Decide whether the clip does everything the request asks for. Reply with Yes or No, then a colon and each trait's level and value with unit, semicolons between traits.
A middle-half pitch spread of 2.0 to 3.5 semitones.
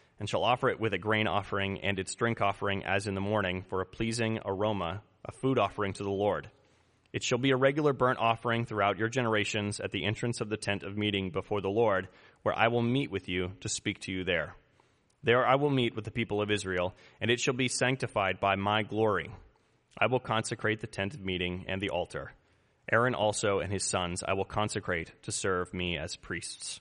Yes: average, 3.0 semitones